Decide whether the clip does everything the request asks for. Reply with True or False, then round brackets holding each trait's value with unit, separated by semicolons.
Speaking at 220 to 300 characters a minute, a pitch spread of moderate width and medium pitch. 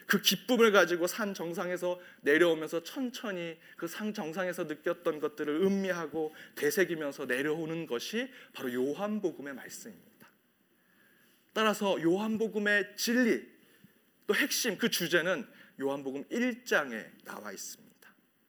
True (285 characters per minute; 4.8 semitones; 180 Hz)